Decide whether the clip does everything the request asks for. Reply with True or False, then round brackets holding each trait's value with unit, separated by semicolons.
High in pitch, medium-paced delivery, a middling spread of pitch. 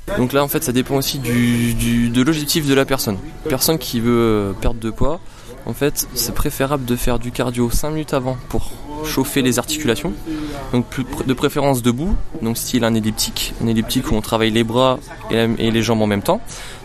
False (125 Hz; 200 wpm; 3.4 semitones)